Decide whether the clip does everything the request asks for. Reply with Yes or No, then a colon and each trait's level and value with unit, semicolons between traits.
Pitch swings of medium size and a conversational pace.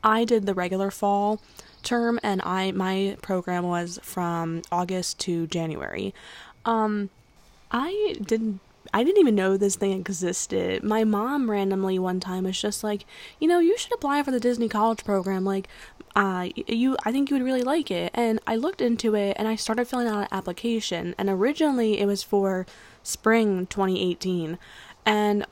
Yes: average, 3.4 semitones; average, 175 wpm